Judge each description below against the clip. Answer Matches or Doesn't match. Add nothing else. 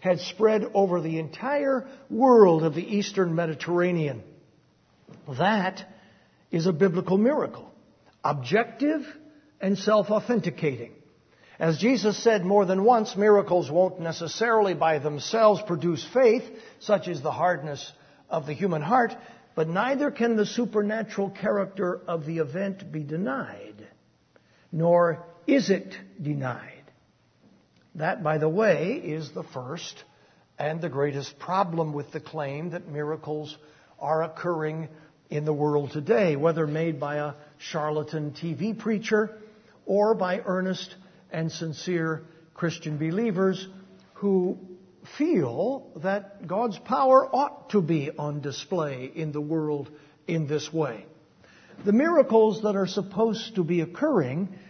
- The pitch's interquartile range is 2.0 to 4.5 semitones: Doesn't match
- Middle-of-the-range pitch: Matches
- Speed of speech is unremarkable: Doesn't match